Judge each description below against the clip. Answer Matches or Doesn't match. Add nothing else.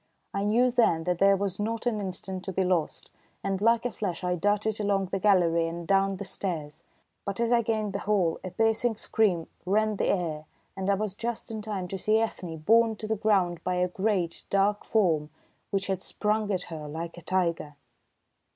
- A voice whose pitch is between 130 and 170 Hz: Doesn't match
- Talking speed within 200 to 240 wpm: Matches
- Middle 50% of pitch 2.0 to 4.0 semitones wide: Matches